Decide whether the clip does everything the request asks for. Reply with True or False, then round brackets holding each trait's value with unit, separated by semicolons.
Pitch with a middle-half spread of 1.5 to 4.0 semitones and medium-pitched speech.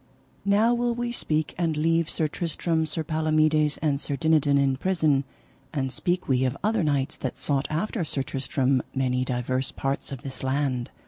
True (3.5 semitones; 150 Hz)